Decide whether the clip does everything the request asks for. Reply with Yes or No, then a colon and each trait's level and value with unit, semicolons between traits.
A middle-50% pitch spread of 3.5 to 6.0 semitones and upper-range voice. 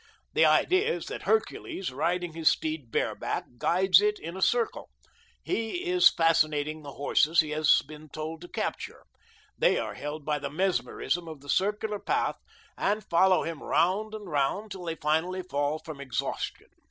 No: average, 4.2 semitones; medium, 165 Hz